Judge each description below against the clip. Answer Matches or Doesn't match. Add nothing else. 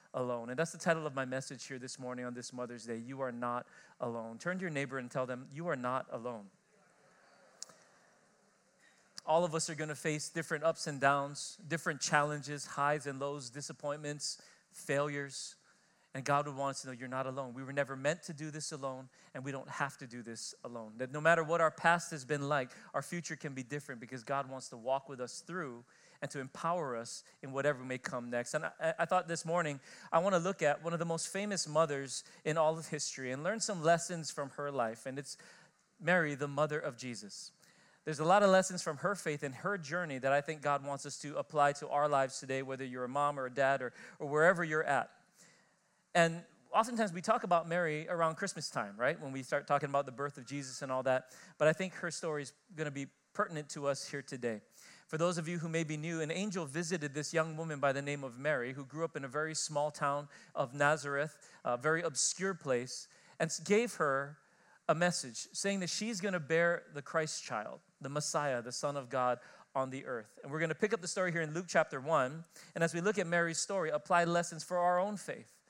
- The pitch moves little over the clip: Doesn't match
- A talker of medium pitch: Matches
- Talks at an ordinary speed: Doesn't match